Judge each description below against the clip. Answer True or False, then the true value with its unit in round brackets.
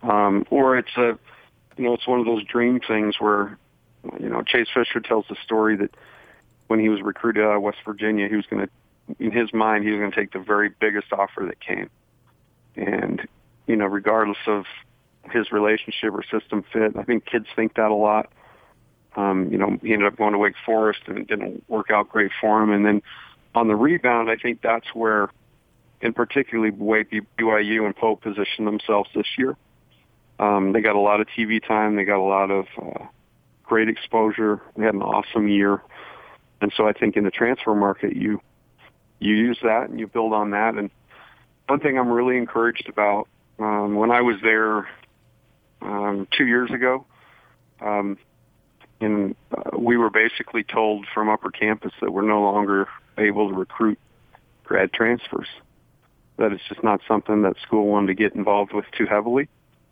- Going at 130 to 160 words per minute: False (185 wpm)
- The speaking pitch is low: True (110 Hz)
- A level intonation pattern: True (1.7 semitones)